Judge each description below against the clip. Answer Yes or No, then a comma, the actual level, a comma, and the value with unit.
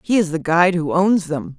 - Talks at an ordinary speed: No, fast, 265 wpm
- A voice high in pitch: No, medium, 175 Hz